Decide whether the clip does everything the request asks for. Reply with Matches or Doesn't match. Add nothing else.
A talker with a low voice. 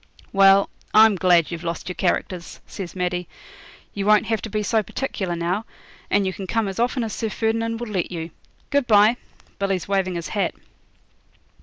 Doesn't match